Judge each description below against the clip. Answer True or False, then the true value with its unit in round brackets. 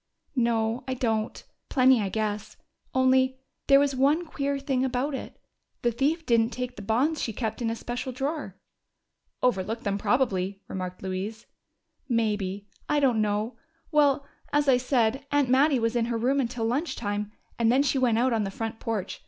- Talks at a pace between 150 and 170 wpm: False (180 wpm)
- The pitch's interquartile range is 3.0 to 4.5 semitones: True (3.5 semitones)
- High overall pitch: True (240 Hz)